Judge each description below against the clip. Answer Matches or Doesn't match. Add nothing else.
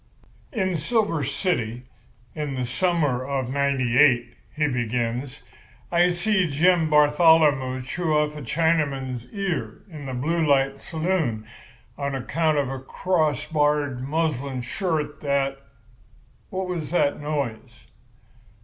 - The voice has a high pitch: Doesn't match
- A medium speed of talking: Doesn't match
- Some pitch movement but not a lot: Matches